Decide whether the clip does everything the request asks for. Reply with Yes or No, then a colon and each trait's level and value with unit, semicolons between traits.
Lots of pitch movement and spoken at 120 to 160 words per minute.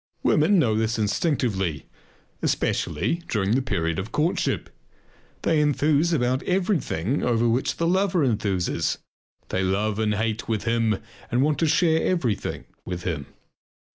Yes: wide, 6.8 semitones; average, 140 wpm